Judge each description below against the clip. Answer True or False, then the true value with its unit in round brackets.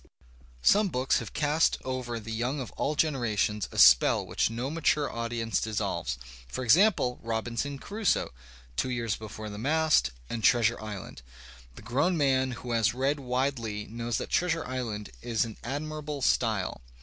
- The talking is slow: False (155 wpm)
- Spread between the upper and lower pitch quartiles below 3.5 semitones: False (4.2 semitones)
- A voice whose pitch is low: True (125 Hz)